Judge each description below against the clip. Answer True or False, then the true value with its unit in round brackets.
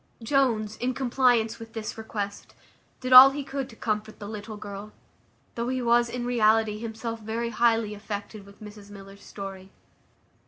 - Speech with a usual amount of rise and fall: False (2.3 semitones)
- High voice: True (220 Hz)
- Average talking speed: True (160 wpm)